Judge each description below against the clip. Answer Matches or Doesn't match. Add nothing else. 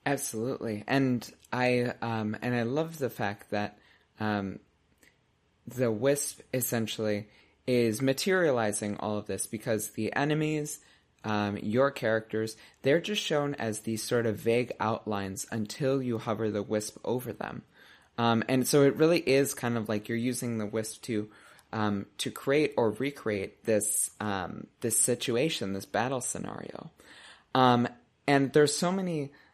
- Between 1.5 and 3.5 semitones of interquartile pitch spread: Doesn't match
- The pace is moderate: Matches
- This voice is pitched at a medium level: Doesn't match